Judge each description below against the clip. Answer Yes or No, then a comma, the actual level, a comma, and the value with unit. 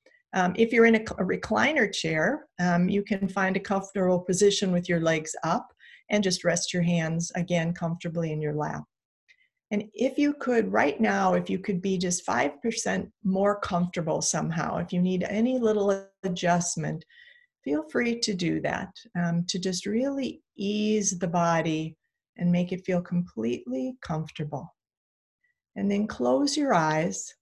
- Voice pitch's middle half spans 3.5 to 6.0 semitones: Yes, average, 3.9 semitones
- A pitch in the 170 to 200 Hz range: Yes, high, 190 Hz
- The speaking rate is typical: Yes, average, 160 wpm